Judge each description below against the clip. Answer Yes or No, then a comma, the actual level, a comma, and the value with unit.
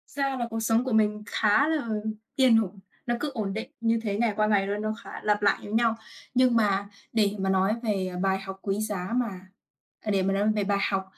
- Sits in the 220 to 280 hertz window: No, high, 210 Hz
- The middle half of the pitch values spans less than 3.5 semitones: Yes, average, 2.7 semitones